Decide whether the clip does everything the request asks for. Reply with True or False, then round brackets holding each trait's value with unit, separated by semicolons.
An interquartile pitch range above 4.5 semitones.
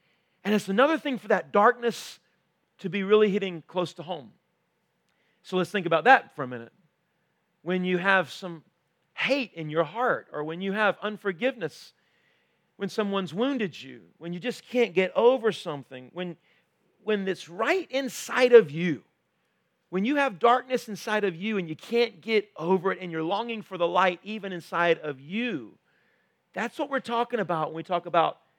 True (5.0 semitones)